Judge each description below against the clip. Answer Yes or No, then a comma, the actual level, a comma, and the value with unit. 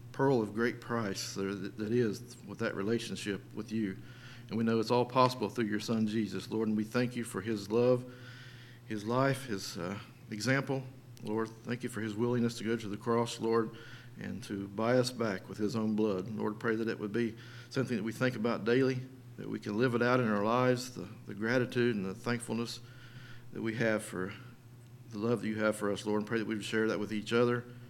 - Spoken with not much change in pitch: Yes, narrow, 2.1 semitones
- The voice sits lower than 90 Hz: No, low, 115 Hz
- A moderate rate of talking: No, fast, 225 wpm